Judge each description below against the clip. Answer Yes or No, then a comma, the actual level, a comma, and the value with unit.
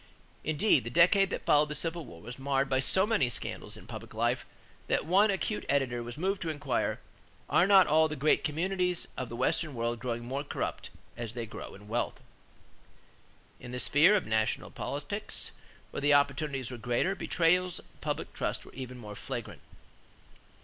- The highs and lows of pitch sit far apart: Yes, wide, 6.1 semitones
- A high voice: No, medium, 140 Hz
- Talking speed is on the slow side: No, average, 180 wpm